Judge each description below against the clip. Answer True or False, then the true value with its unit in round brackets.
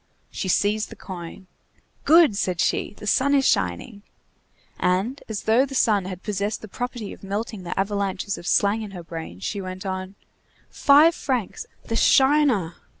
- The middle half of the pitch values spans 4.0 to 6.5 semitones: True (4.8 semitones)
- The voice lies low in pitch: False (205 Hz)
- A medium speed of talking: True (165 wpm)